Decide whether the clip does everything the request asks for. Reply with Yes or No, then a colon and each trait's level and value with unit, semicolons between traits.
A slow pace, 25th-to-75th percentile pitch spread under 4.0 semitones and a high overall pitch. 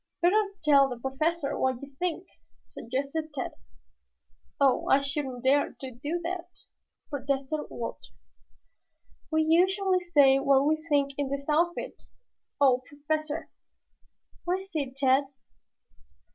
Yes: slow, 120 wpm; average, 3.5 semitones; very high, 285 Hz